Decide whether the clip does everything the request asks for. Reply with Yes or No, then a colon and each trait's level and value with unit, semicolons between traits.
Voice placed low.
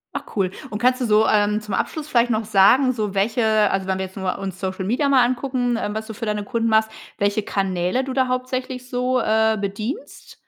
No: high, 220 Hz